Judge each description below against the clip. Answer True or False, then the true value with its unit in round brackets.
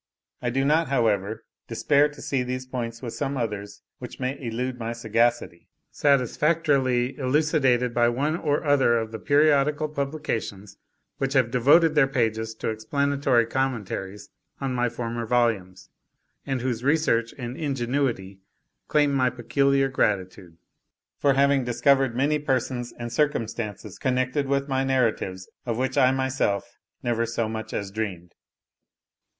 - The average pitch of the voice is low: True (125 Hz)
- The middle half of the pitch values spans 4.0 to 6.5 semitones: False (3.3 semitones)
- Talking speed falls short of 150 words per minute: True (140 wpm)